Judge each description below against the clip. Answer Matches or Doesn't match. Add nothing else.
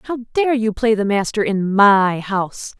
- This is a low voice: Doesn't match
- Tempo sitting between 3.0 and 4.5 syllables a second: Matches